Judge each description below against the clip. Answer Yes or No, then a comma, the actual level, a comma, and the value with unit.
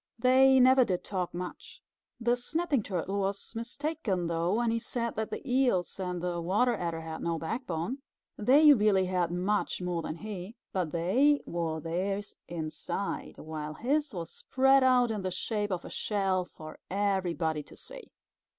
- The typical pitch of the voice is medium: No, high, 195 Hz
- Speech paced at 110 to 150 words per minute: No, average, 165 wpm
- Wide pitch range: Yes, wide, 5.9 semitones